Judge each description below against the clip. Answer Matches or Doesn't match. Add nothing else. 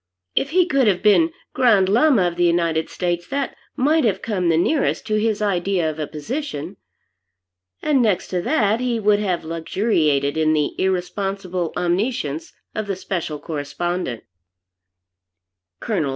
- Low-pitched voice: Doesn't match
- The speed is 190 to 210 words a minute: Doesn't match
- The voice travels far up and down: Doesn't match